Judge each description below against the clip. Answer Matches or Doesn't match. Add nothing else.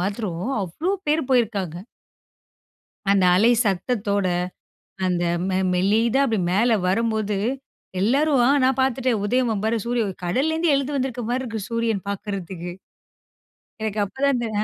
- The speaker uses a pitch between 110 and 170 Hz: Doesn't match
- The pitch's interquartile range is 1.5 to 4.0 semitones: Doesn't match